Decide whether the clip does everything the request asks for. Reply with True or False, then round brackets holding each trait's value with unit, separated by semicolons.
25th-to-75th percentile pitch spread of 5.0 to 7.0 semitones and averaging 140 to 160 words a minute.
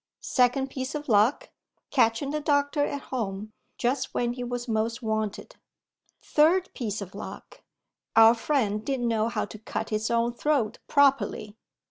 False (4.4 semitones; 150 wpm)